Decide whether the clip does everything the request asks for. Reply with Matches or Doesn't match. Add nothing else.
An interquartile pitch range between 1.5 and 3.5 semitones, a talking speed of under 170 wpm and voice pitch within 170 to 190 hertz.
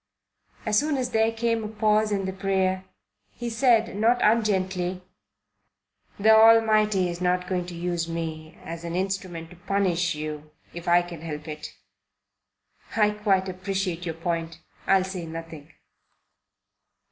Doesn't match